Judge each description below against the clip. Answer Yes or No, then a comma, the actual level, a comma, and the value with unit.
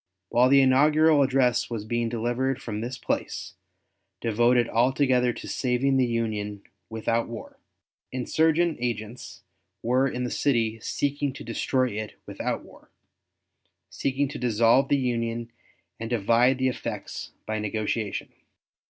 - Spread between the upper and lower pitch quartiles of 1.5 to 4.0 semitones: Yes, narrow, 2.5 semitones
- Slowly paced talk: Yes, slow, 130 wpm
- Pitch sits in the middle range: No, low, 120 Hz